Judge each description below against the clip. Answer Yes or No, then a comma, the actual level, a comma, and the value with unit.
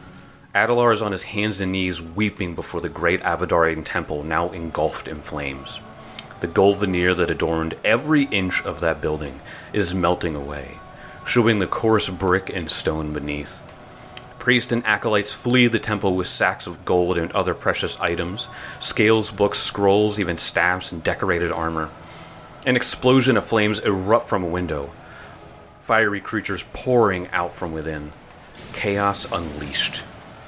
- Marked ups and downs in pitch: No, average, 4.4 semitones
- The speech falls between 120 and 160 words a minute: Yes, average, 150 wpm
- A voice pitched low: Yes, very low, 95 Hz